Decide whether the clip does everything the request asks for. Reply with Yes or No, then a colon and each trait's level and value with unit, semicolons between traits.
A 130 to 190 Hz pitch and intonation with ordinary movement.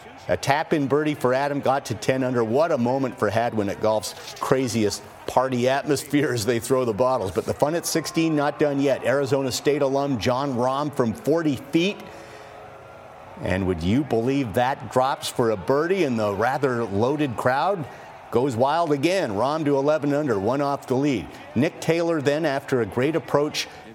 Yes: low, 135 Hz; average, 3.1 semitones